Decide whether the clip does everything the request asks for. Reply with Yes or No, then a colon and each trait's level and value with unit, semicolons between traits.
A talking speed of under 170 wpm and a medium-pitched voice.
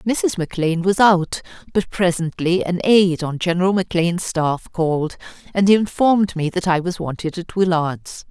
Yes: average, 160 wpm; medium, 180 Hz